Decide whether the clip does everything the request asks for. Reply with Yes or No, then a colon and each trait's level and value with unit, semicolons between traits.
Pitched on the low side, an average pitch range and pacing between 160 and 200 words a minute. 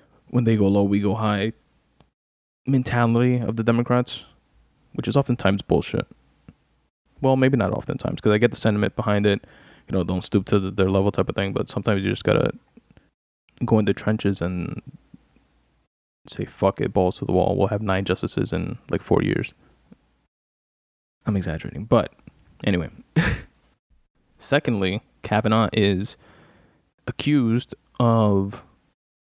No: low, 105 Hz; average, 4.0 semitones; average, 145 wpm